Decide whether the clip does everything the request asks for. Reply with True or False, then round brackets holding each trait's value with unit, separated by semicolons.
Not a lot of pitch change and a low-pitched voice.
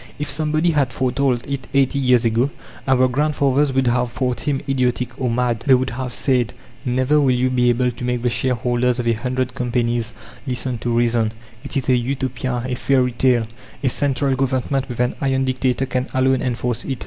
True (1.6 semitones; 125 Hz)